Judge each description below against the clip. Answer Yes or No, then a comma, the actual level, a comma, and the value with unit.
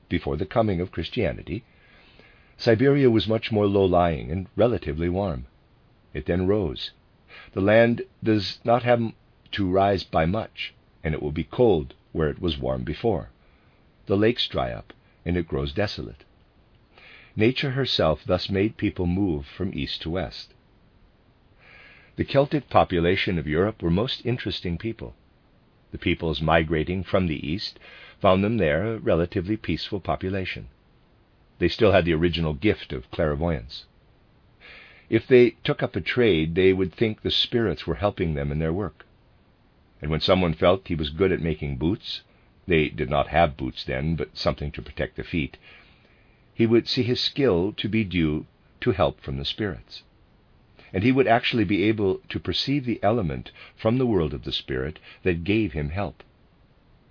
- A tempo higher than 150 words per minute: Yes, average, 165 wpm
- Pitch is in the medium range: No, very low, 95 Hz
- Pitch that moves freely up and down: Yes, wide, 5.7 semitones